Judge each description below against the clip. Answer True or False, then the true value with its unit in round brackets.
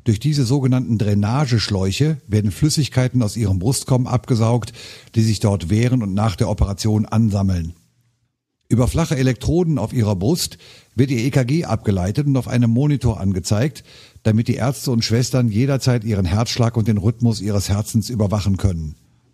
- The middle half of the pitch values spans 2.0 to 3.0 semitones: False (3.4 semitones)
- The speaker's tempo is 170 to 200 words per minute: False (150 wpm)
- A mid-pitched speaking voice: False (115 Hz)